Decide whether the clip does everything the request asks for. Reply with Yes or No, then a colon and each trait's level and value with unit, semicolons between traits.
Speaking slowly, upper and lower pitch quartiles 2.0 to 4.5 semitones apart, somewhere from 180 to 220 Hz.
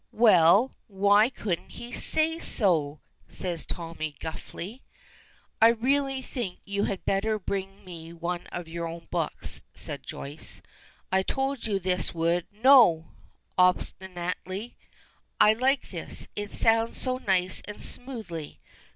No: slow, 130 wpm; average, 5.0 semitones; high, 190 Hz